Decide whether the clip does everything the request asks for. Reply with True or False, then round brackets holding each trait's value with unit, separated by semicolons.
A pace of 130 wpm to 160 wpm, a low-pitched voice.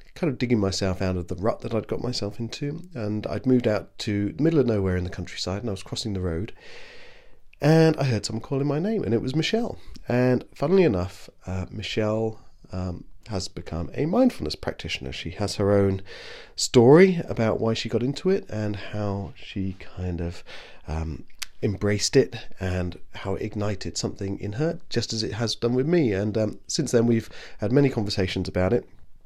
False (195 wpm; 105 Hz)